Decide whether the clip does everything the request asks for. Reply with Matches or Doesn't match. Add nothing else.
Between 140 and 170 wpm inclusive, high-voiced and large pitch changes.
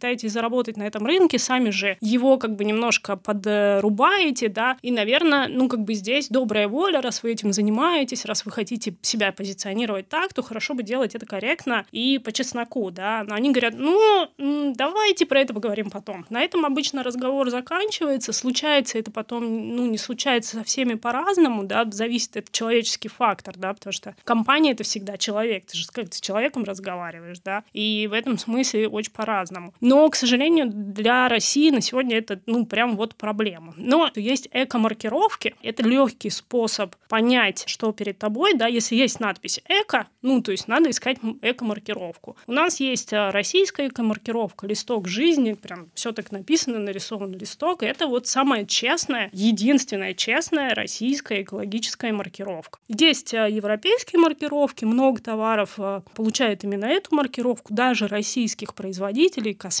Doesn't match